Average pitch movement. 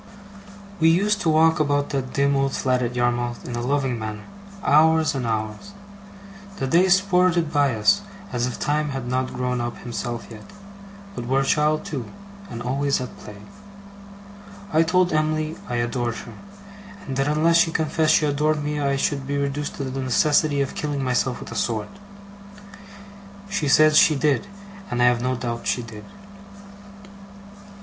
Yes: average, 4.0 semitones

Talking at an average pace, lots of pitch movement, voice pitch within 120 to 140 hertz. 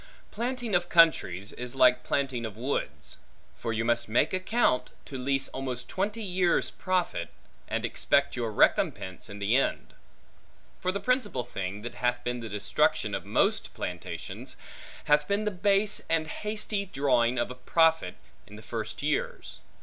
Yes: average, 155 wpm; wide, 7.7 semitones; low, 135 Hz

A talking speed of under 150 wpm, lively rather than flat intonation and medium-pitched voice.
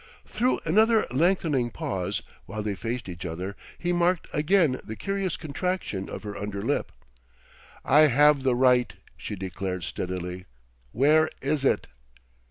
No: average, 140 wpm; wide, 8.8 semitones; low, 130 Hz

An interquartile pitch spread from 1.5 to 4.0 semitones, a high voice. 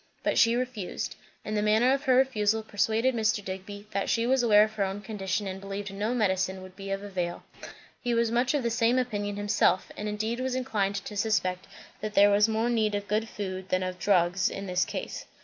Yes: average, 2.8 semitones; high, 210 Hz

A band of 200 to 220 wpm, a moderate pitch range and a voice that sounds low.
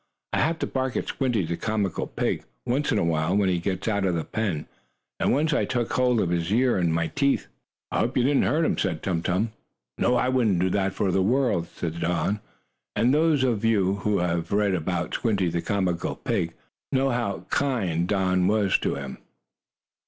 No: fast, 205 wpm; wide, 5.9 semitones; low, 100 Hz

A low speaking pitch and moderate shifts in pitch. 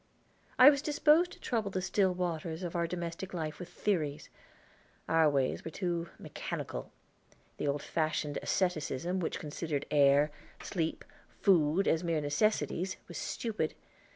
No: medium, 170 Hz; average, 3.5 semitones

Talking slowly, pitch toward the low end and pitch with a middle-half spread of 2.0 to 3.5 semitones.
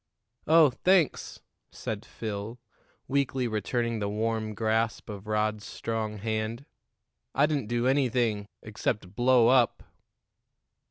Yes: slow, 110 wpm; low, 115 Hz; average, 2.9 semitones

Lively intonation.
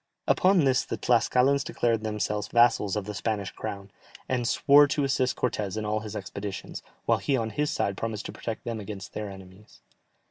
No: average, 3.6 semitones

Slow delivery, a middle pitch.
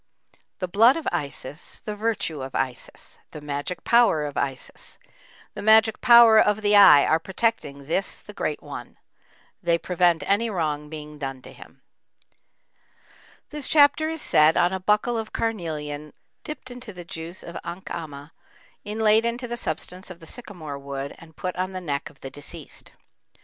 No: average, 165 wpm; medium, 180 Hz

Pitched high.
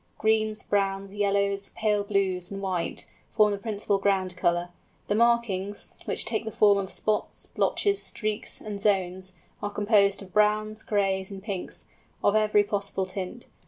Yes: high, 200 Hz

